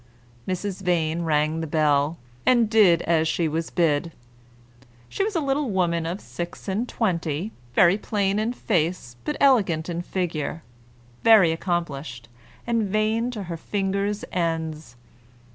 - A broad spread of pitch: No, average, 4.5 semitones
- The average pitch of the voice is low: No, medium, 175 Hz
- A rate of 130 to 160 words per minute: Yes, average, 140 wpm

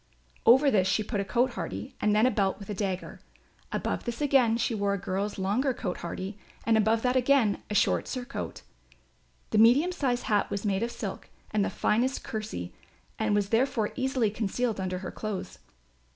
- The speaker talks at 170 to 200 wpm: Yes, average, 190 wpm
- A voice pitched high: Yes, high, 220 Hz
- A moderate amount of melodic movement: Yes, average, 3.8 semitones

